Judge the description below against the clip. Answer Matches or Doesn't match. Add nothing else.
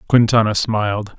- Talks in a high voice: Doesn't match